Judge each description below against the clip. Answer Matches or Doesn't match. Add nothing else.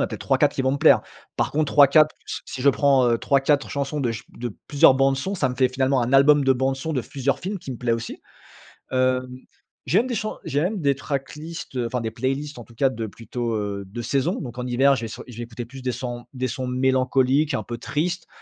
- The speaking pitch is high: Doesn't match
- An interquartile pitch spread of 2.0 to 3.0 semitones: Matches